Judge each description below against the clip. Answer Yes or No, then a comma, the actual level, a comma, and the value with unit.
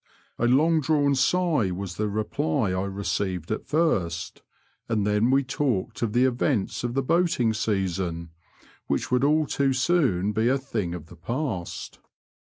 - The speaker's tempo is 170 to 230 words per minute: No, average, 155 wpm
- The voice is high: No, low, 115 Hz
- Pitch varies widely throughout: Yes, wide, 6.2 semitones